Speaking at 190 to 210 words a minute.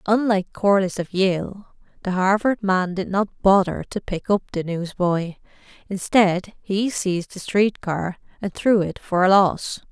No: average, 165 wpm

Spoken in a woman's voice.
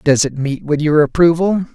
No: male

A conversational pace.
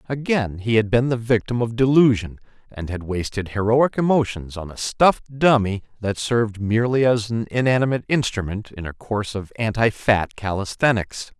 Yes: average, 165 wpm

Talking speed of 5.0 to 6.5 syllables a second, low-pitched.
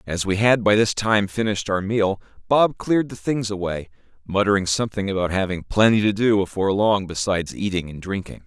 Yes: 5.7 syllables/s; low, 100 Hz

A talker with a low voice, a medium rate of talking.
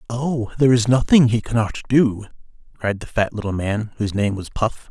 Yes: low, 115 Hz; average, 195 wpm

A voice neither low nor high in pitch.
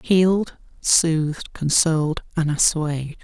Yes: medium, 160 Hz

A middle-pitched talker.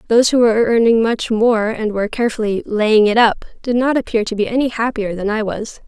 No: high, 225 Hz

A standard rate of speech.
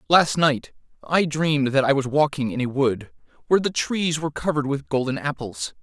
Yes: average, 195 wpm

